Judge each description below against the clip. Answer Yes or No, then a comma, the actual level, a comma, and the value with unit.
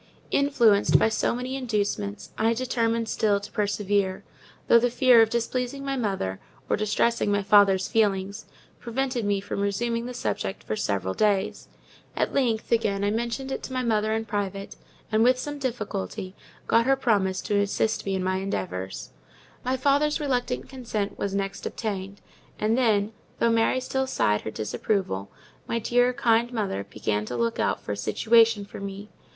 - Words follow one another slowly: No, average, 170 wpm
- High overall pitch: Yes, high, 215 Hz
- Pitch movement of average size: Yes, average, 3.6 semitones